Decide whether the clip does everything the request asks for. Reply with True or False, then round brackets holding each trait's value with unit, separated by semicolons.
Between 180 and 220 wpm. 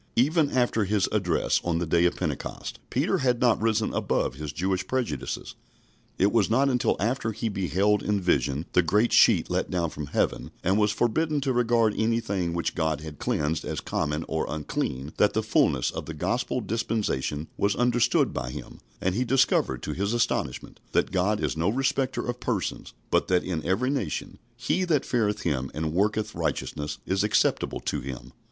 True (185 wpm)